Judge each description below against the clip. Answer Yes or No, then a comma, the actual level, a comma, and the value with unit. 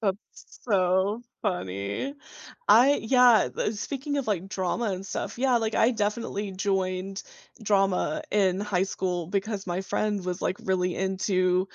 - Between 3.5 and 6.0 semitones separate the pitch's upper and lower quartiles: No, average, 2.8 semitones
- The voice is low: No, high, 195 Hz